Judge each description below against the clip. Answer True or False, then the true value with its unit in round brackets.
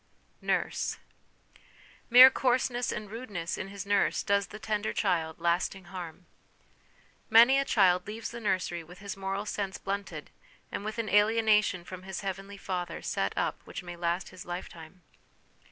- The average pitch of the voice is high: True (195 Hz)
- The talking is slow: False (155 wpm)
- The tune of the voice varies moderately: True (3.2 semitones)